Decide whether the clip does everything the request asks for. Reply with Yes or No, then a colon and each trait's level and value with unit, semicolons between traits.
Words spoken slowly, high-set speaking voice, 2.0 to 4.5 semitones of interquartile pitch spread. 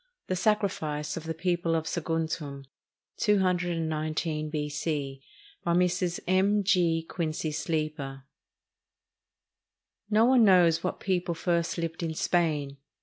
No: slow, 110 wpm; medium, 165 Hz; average, 2.8 semitones